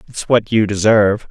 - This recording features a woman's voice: No, male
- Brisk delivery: No, average, 185 wpm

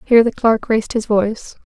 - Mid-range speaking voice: No, high, 220 Hz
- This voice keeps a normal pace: No, fast, 215 wpm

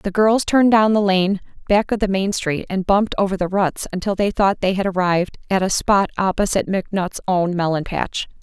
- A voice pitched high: Yes, high, 195 Hz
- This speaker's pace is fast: Yes, fast, 215 wpm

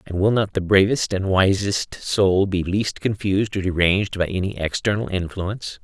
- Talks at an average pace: Yes, average, 175 wpm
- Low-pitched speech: Yes, very low, 95 Hz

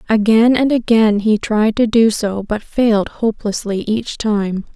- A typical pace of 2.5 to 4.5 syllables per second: Yes, 4.2 syllables/s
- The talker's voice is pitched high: Yes, high, 215 Hz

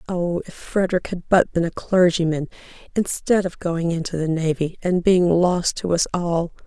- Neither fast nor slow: Yes, average, 180 wpm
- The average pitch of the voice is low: No, medium, 175 Hz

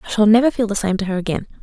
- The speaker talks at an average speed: No, fast, 335 wpm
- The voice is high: Yes, high, 210 Hz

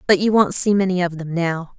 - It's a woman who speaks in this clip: Yes, female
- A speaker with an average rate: No, fast, 270 wpm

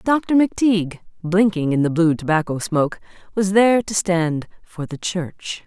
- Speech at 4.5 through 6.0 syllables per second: Yes, 4.8 syllables/s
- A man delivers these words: No, female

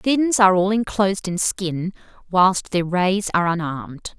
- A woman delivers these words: Yes, female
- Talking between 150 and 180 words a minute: Yes, average, 170 wpm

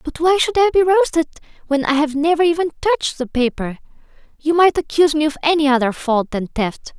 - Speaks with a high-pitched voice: Yes, very high, 305 Hz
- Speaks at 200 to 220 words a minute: Yes, fast, 205 wpm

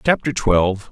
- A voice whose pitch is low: Yes, low, 115 Hz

